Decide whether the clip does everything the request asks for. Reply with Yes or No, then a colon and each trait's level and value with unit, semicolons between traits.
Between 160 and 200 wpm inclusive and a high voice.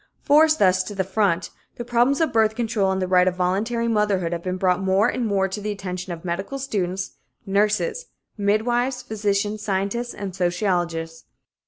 Yes: average, 175 wpm; high, 200 Hz